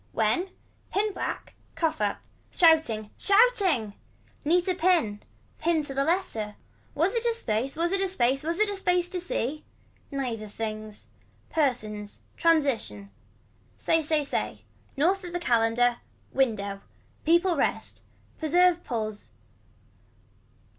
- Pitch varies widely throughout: Yes, wide, 7.9 semitones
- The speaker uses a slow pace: Yes, slow, 125 wpm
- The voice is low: No, very high, 305 Hz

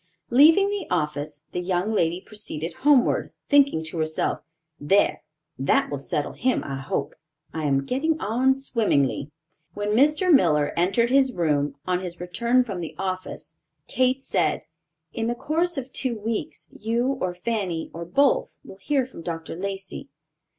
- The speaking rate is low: No, average, 155 wpm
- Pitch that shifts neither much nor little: No, wide, 7.9 semitones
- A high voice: Yes, high, 195 Hz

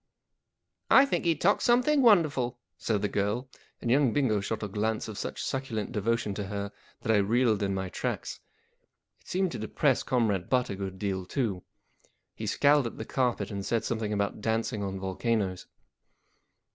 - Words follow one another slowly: No, average, 185 wpm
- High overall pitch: No, low, 110 Hz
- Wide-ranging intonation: No, average, 4.4 semitones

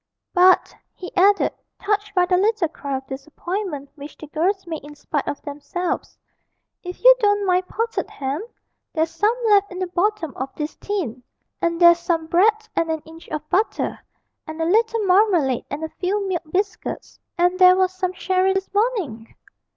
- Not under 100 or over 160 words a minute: No, average, 175 wpm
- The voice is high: Yes, very high, 360 Hz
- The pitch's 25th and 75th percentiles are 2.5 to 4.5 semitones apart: Yes, average, 4.1 semitones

